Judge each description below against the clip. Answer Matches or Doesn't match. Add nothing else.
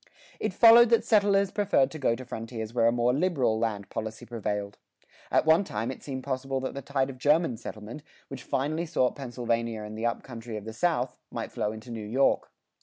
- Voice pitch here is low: Matches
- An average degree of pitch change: Matches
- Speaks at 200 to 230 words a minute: Matches